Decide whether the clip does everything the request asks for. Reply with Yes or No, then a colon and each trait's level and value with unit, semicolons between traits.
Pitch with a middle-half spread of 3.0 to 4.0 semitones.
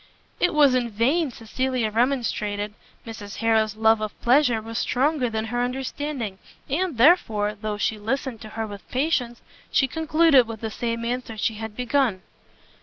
Yes: average, 3.5 semitones